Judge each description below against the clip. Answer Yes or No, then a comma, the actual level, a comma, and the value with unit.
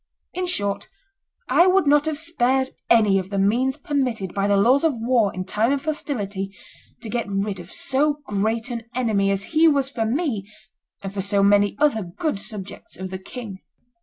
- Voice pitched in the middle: No, high, 225 Hz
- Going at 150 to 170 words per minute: No, average, 190 wpm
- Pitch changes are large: Yes, wide, 5.7 semitones